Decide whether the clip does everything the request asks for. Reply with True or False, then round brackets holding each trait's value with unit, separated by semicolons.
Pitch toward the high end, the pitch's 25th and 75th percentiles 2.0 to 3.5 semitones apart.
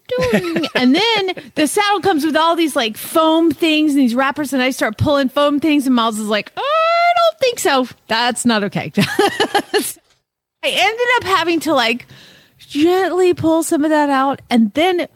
False (315 Hz; 5.4 semitones)